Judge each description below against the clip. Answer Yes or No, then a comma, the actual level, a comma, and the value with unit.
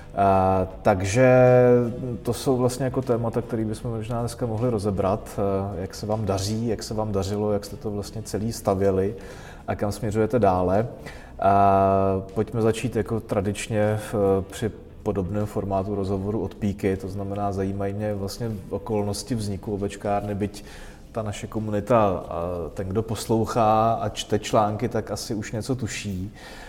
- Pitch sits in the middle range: No, low, 105 Hz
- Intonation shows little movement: Yes, narrow, 2.2 semitones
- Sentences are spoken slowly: No, average, 155 wpm